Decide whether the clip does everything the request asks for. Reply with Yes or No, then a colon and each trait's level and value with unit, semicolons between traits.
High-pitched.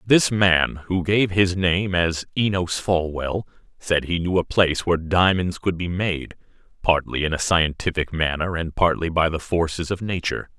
No: very low, 85 Hz